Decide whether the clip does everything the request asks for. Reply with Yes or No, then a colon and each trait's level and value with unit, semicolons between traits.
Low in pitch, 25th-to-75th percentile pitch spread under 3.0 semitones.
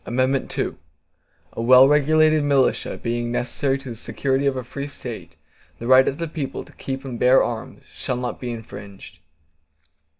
Yes: low, 130 Hz; narrow, 2.5 semitones